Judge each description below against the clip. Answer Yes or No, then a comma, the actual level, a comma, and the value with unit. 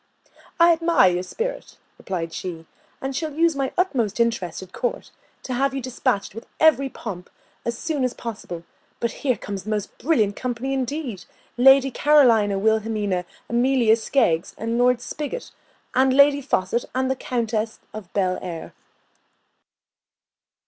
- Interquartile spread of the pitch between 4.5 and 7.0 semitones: Yes, average, 4.9 semitones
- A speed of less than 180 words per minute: Yes, average, 140 wpm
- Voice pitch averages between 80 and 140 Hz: No, high, 235 Hz